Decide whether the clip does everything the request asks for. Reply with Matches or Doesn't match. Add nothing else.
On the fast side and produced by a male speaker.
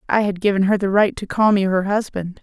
Doesn't match